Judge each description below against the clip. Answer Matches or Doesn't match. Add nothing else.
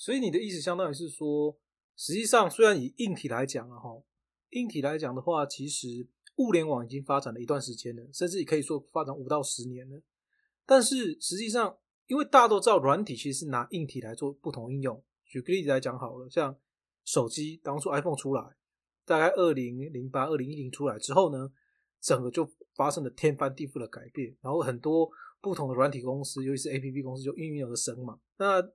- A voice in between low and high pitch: Matches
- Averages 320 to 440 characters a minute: Matches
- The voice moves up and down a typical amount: Matches